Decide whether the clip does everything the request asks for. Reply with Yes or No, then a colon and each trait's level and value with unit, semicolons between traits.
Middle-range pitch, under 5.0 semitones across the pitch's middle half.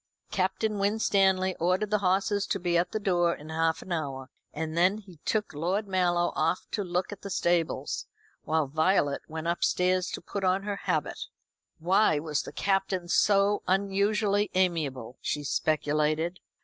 Yes: medium, 180 Hz; average, 3.5 semitones